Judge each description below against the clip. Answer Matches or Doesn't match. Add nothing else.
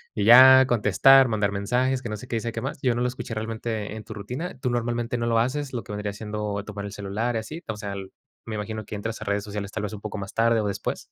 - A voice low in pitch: Matches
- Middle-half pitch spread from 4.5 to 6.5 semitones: Doesn't match